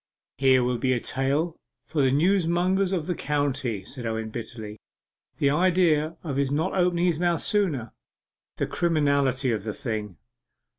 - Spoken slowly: No, average, 155 wpm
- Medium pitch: Yes, medium, 145 Hz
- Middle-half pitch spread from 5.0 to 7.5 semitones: Yes, wide, 5.5 semitones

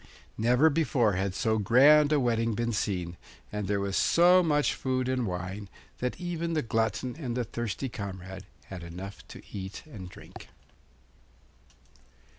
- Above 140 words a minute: Yes, average, 150 wpm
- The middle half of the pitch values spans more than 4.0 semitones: Yes, wide, 5.5 semitones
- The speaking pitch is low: Yes, low, 115 Hz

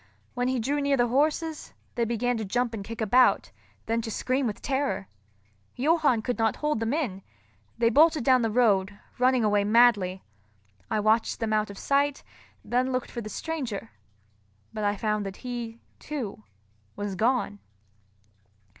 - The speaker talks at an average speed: Yes, average, 165 wpm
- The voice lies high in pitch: Yes, high, 235 Hz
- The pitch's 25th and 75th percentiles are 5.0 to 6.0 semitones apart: No, average, 3.5 semitones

